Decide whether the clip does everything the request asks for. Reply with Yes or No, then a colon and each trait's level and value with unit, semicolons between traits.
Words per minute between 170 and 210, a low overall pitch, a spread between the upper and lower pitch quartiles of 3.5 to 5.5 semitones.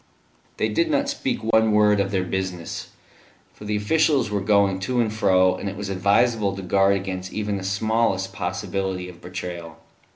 No: average, 175 wpm; low, 100 Hz; narrow, 2.5 semitones